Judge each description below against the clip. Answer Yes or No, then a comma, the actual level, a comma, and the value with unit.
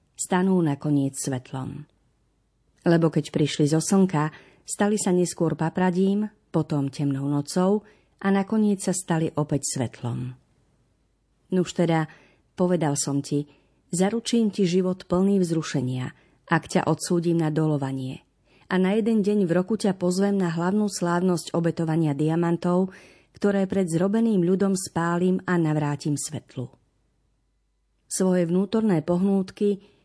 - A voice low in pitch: No, medium, 170 Hz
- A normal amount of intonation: Yes, average, 4.4 semitones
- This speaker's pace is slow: No, average, 120 wpm